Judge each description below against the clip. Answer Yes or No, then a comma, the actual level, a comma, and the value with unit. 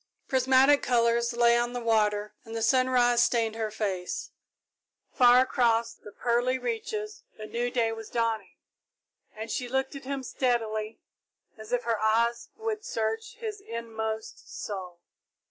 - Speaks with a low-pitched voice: No, high, 235 Hz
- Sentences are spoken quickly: No, average, 145 wpm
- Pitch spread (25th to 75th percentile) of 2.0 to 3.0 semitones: Yes, narrow, 2.5 semitones